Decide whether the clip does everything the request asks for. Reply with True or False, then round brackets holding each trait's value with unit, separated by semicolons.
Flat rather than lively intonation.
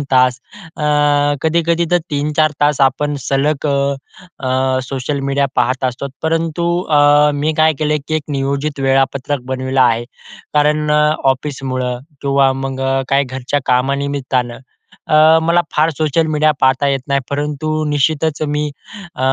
True (2.3 semitones)